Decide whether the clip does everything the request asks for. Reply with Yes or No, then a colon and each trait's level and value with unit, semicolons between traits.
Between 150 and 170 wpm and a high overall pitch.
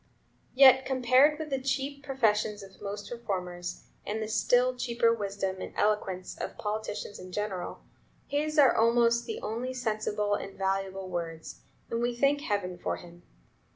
Yes: average, 155 wpm; high, 215 Hz